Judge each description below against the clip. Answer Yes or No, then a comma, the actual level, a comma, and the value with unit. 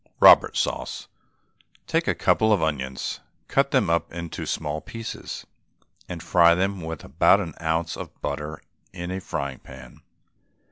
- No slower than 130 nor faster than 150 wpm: Yes, average, 145 wpm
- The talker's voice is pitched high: No, very low, 85 Hz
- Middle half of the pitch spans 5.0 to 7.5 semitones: No, average, 3.8 semitones